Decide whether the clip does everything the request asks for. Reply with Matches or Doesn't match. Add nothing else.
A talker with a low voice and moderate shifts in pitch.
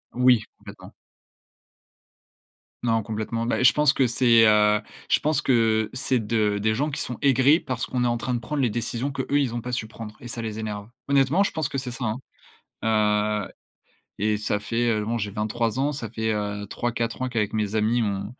Matches